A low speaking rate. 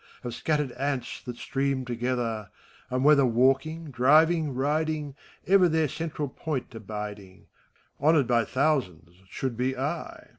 Yes: slow, 125 wpm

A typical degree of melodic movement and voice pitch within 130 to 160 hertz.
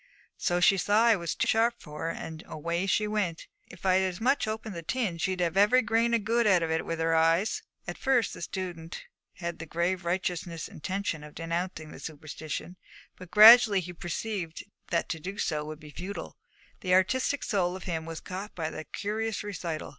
No: average, 4.1 semitones; medium, 180 Hz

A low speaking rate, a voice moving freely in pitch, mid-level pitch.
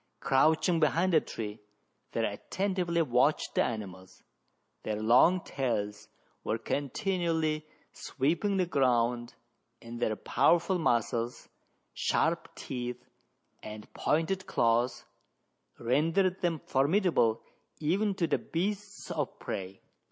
Yes: slow, 105 wpm; wide, 6.7 semitones; medium, 145 Hz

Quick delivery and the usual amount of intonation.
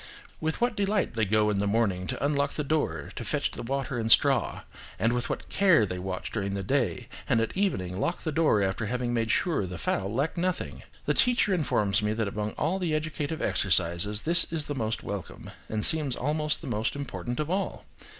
No: fast, 210 wpm; wide, 7.3 semitones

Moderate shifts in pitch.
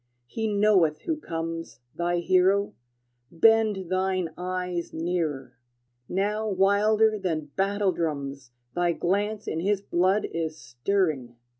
Yes: average, 3.7 semitones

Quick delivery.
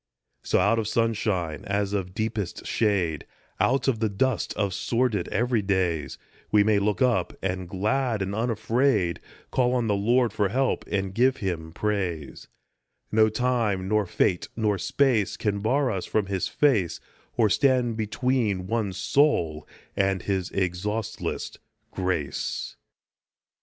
No: average, 140 wpm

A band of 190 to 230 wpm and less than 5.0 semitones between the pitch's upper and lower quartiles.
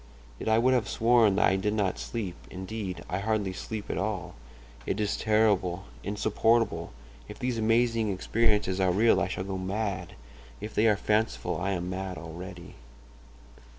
No: average, 160 wpm; average, 2.8 semitones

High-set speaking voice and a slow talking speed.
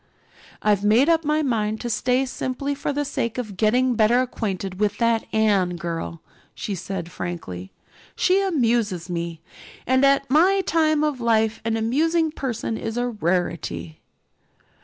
No: high, 230 Hz; average, 150 wpm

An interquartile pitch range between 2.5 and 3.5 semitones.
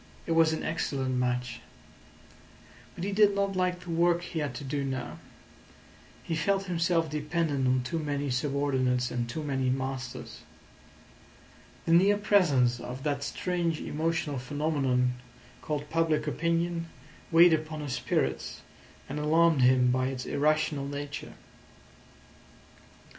No: average, 4.2 semitones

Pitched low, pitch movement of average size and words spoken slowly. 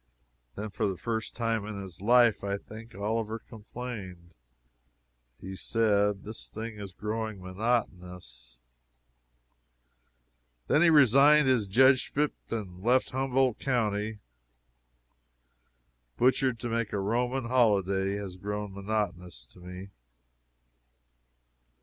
Yes: low, 105 Hz; average, 3.7 semitones; slow, 105 wpm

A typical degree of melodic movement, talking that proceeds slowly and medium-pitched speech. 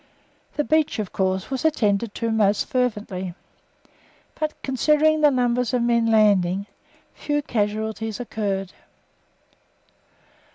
No: average, 4.3 semitones; slow, 110 wpm; high, 225 Hz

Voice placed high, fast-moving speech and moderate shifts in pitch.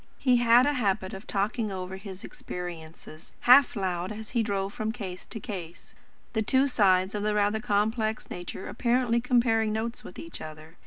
No: high, 210 Hz; average, 175 wpm; average, 3.8 semitones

